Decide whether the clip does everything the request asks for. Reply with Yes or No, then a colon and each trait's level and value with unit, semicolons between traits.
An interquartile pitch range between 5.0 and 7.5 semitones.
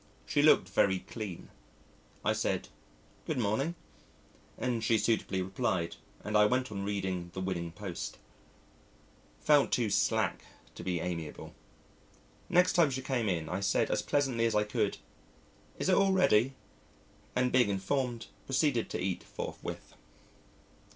Yes: wide, 5.4 semitones